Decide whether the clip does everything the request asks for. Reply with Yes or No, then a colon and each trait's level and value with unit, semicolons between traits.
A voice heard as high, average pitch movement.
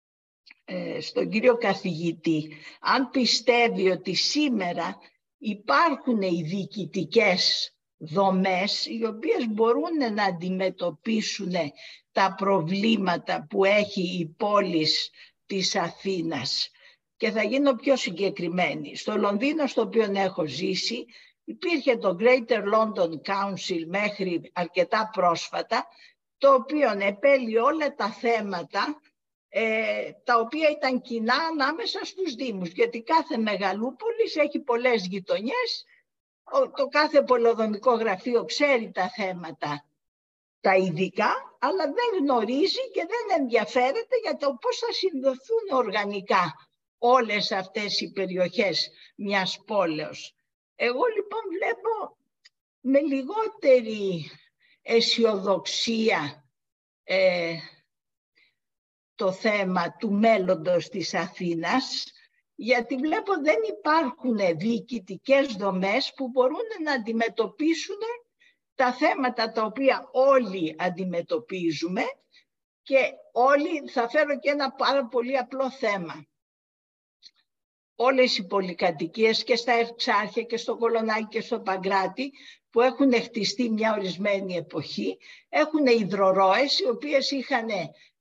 No: high, 230 Hz; wide, 6.1 semitones